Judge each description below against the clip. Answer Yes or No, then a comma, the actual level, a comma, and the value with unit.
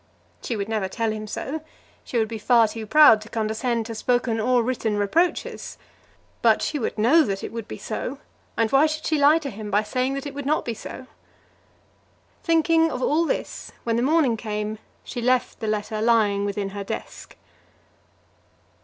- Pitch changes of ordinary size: Yes, average, 4.3 semitones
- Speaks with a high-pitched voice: Yes, high, 230 Hz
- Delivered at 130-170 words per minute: No, average, 190 wpm